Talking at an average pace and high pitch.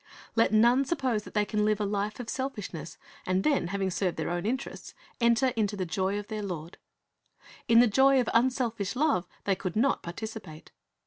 Yes: average, 190 wpm; high, 215 Hz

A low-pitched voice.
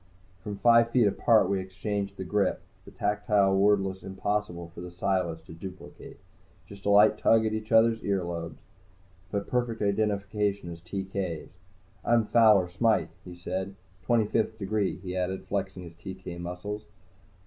Yes: low, 100 Hz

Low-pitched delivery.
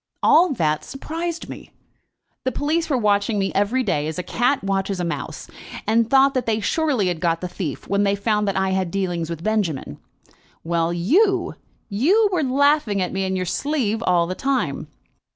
No: high, 205 Hz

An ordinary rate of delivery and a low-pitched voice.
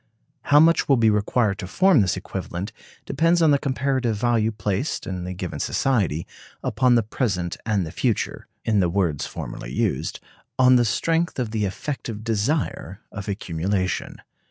Yes: average, 160 wpm; low, 110 Hz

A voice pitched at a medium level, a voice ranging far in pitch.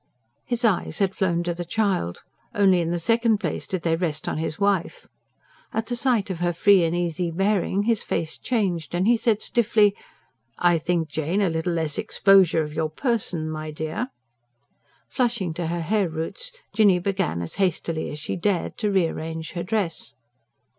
No: medium, 180 Hz; average, 4.0 semitones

